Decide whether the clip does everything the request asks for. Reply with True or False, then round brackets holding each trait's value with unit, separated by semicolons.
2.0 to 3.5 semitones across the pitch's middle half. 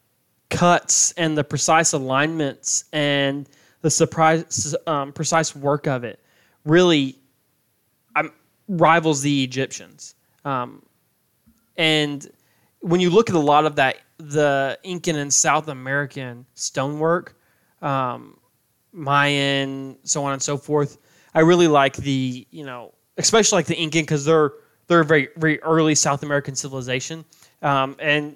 True (2.9 semitones)